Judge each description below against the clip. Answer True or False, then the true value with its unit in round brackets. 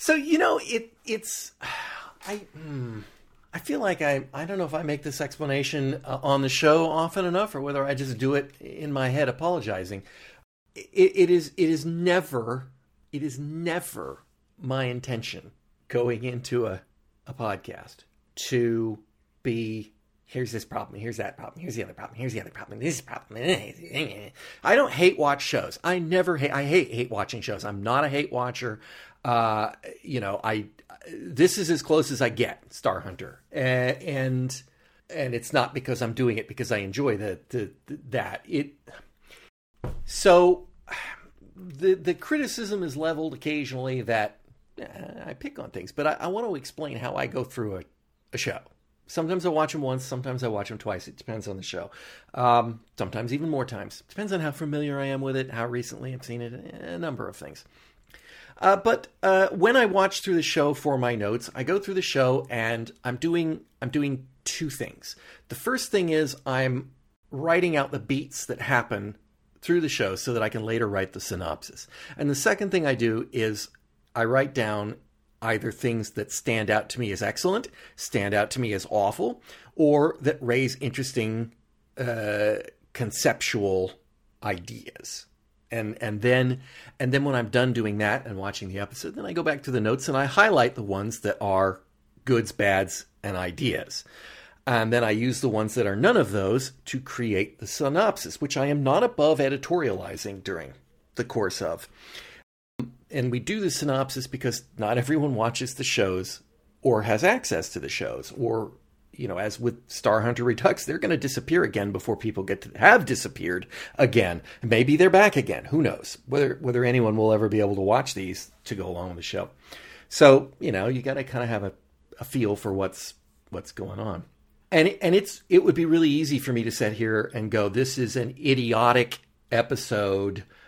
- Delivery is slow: False (185 wpm)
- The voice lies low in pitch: True (125 Hz)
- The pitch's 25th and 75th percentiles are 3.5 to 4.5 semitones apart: False (5.2 semitones)